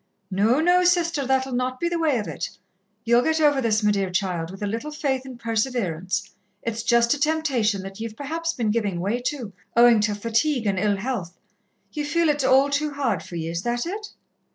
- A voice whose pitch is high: Yes, high, 240 Hz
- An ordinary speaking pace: No, fast, 210 wpm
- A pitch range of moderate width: No, wide, 6.0 semitones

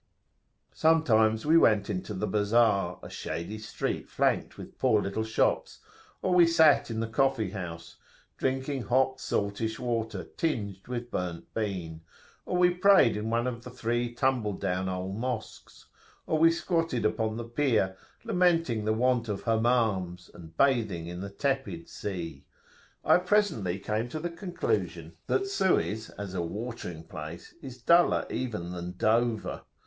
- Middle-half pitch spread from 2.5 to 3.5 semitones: No, average, 5.3 semitones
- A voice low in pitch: Yes, low, 115 Hz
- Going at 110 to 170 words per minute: Yes, average, 150 wpm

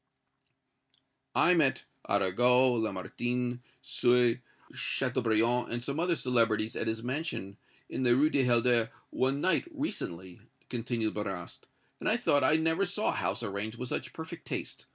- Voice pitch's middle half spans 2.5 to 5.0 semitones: Yes, average, 3.7 semitones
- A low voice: Yes, low, 125 Hz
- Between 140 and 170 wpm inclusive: Yes, average, 145 wpm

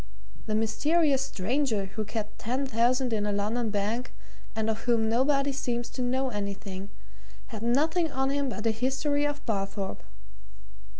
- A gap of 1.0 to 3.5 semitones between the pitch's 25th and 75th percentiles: No, average, 4.0 semitones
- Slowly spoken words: No, average, 155 wpm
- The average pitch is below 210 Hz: No, high, 235 Hz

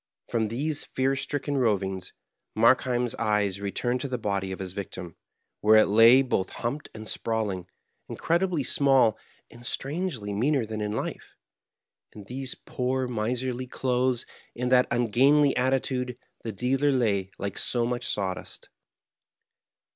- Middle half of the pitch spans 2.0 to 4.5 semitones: Yes, average, 3.8 semitones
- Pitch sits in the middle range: No, low, 120 Hz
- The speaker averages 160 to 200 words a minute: No, average, 140 wpm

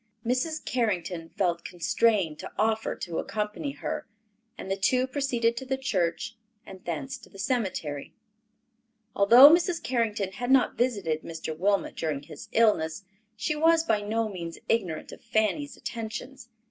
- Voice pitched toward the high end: Yes, high, 220 Hz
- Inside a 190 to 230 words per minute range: No, average, 145 wpm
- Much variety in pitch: Yes, wide, 5.8 semitones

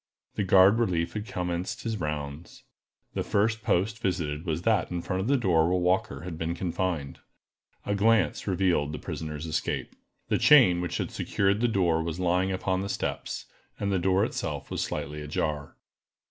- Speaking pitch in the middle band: No, very low, 90 Hz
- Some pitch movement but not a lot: Yes, average, 3.5 semitones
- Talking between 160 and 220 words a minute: Yes, average, 175 wpm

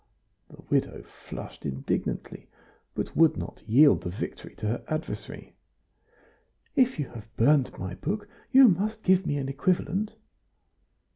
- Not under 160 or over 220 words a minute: No, slow, 135 wpm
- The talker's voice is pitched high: No, medium, 155 Hz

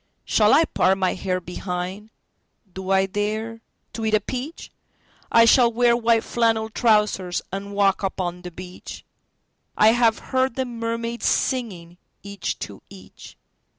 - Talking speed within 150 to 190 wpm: No, slow, 135 wpm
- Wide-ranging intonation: No, average, 3.7 semitones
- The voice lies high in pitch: Yes, high, 210 Hz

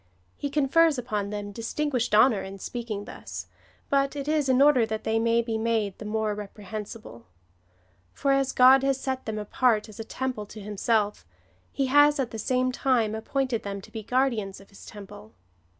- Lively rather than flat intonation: No, average, 4.0 semitones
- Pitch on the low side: No, high, 230 Hz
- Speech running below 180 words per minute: No, average, 185 wpm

